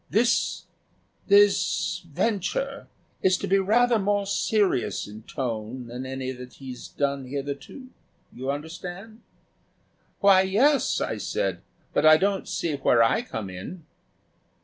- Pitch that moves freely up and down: Yes, wide, 7.7 semitones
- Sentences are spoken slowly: Yes, slow, 125 wpm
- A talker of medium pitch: Yes, medium, 170 Hz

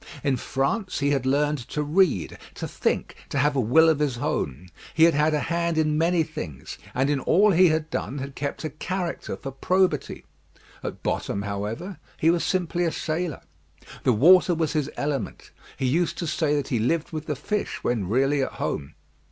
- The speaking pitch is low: No, medium, 150 Hz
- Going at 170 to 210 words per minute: Yes, average, 195 wpm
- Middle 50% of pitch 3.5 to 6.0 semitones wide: Yes, average, 3.8 semitones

